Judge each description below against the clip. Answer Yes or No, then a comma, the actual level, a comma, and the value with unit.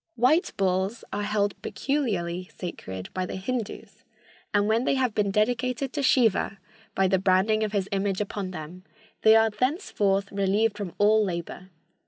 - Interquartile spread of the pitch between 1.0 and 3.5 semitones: Yes, average, 3.0 semitones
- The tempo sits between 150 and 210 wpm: Yes, average, 160 wpm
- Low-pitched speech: No, high, 205 Hz